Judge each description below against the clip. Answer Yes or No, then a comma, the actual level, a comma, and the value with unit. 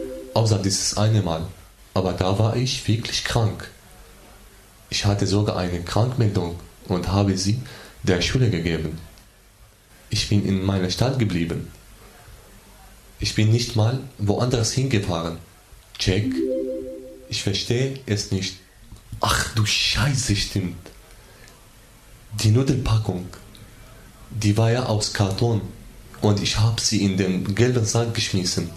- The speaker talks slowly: Yes, slow, 120 wpm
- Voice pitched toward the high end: No, low, 105 Hz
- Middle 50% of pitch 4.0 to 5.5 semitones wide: No, average, 3.3 semitones